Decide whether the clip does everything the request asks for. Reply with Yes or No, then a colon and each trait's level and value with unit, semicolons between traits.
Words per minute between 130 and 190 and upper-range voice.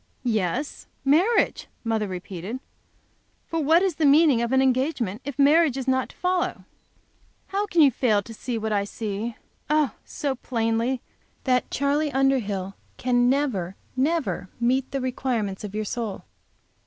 Yes: average, 150 wpm; very high, 255 Hz